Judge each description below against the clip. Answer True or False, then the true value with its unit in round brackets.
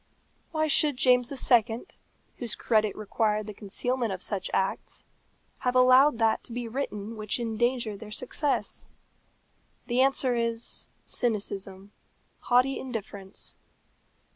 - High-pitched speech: True (230 Hz)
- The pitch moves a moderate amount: True (3.1 semitones)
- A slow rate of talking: True (115 wpm)